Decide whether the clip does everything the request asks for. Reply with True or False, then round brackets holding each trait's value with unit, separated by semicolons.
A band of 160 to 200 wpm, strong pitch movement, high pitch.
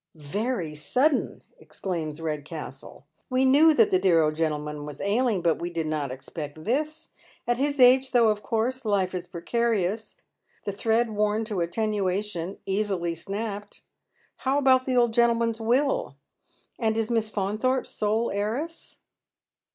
False (150 wpm; 5.8 semitones; 210 Hz)